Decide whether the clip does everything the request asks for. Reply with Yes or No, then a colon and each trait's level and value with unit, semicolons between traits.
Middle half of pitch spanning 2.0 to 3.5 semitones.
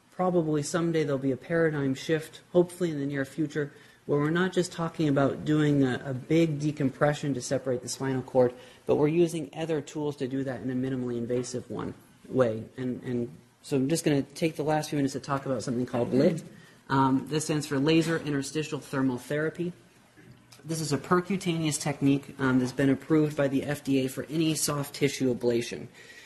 Yes: average, 3.2 semitones